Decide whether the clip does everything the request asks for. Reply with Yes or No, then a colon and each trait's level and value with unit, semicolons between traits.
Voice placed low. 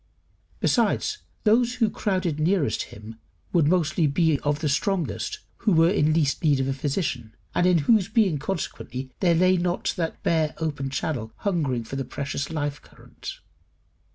No: medium, 155 Hz